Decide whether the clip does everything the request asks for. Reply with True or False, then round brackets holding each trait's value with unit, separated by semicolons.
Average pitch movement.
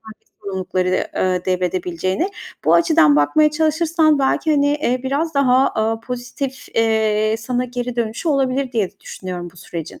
False (7.0 semitones)